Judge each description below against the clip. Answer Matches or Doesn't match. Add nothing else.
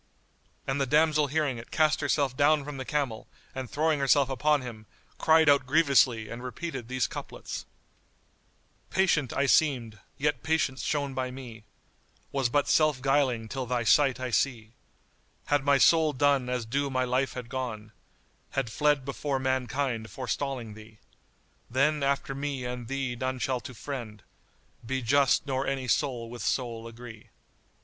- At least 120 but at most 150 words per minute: Doesn't match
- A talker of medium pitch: Doesn't match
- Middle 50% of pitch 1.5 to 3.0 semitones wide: Matches